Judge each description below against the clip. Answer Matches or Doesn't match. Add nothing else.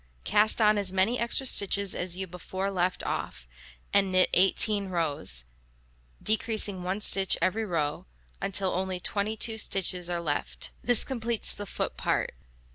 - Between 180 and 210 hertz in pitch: Matches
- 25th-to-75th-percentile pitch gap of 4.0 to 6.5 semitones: Doesn't match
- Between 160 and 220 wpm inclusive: Doesn't match